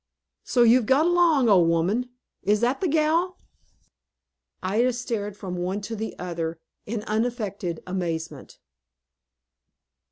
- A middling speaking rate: No, slow, 120 wpm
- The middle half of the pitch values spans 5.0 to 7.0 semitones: Yes, wide, 5.5 semitones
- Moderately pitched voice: No, high, 215 Hz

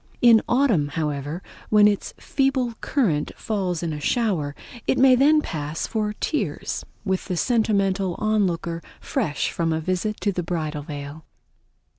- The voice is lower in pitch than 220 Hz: Yes, medium, 185 Hz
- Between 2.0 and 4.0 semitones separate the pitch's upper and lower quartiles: No, wide, 5.6 semitones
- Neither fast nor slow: Yes, average, 145 wpm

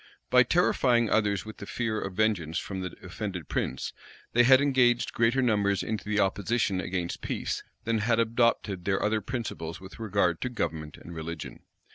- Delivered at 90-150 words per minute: No, average, 170 wpm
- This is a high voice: No, low, 105 Hz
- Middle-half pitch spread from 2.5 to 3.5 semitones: No, average, 4.3 semitones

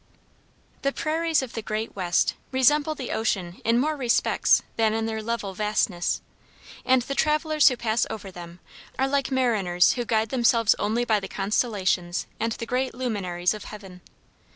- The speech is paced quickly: No, average, 165 wpm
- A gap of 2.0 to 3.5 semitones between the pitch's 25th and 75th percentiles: No, average, 4.4 semitones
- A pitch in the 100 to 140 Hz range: No, high, 225 Hz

